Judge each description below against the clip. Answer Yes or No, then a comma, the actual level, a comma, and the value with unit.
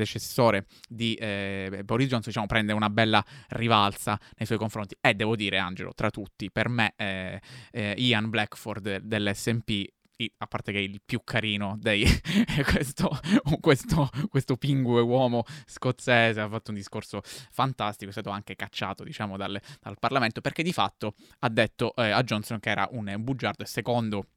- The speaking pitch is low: Yes, low, 110 Hz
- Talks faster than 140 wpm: Yes, fast, 170 wpm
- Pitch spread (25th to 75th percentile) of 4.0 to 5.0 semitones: No, average, 3.2 semitones